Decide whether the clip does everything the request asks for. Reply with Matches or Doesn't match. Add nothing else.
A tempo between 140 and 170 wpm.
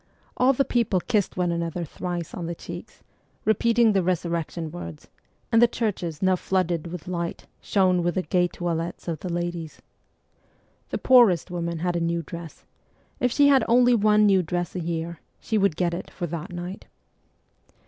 Doesn't match